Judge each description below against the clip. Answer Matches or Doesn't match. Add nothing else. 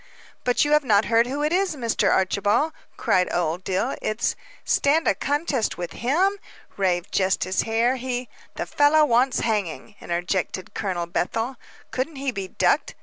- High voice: Matches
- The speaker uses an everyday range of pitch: Doesn't match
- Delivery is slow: Doesn't match